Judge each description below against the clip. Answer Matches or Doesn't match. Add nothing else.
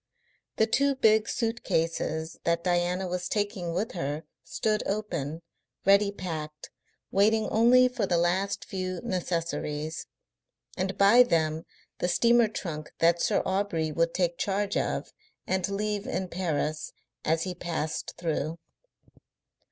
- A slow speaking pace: Matches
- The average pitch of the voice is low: Doesn't match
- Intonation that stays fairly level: Doesn't match